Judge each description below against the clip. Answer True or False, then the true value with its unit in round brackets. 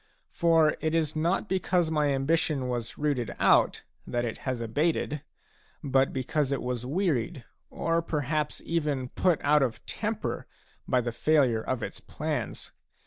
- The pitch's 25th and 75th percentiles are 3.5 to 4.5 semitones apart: True (4.1 semitones)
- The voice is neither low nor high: True (145 Hz)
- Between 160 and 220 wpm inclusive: False (145 wpm)